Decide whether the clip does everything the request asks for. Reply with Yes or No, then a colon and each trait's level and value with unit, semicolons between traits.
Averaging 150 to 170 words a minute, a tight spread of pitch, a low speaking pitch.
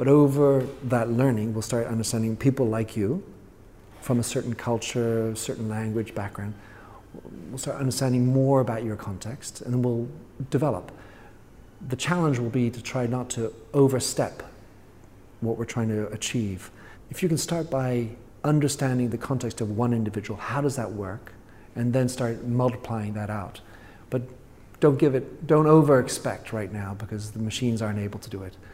No: average, 165 wpm; average, 3.4 semitones; low, 115 Hz